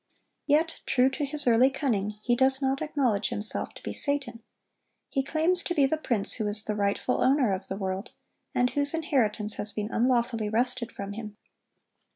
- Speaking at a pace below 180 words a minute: No, average, 185 wpm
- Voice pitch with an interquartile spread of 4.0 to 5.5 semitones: Yes, average, 4.9 semitones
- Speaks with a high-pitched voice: Yes, high, 245 Hz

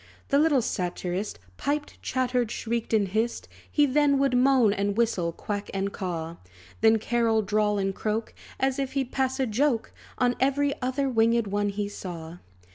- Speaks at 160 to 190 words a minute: Yes, average, 165 wpm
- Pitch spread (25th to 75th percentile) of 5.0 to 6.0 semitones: No, average, 4.5 semitones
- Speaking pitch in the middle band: No, high, 230 Hz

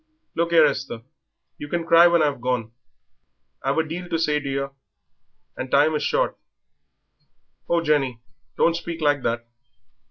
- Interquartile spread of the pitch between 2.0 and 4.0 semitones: Yes, average, 3.6 semitones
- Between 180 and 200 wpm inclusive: No, average, 155 wpm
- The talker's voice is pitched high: No, medium, 150 Hz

